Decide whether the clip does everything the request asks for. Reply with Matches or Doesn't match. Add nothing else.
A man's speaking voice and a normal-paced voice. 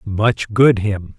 Matches